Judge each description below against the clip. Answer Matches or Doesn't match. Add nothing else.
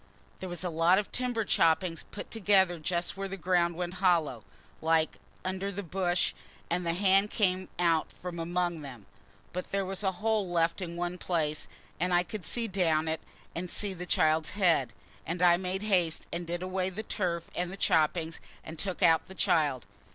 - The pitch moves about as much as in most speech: Doesn't match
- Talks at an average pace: Matches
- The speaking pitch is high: Doesn't match